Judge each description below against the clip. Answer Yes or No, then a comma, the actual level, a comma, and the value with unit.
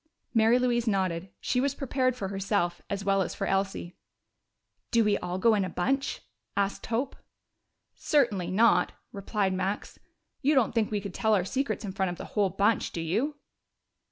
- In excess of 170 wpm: Yes, average, 185 wpm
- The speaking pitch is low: No, high, 205 Hz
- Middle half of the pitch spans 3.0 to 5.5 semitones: Yes, average, 3.8 semitones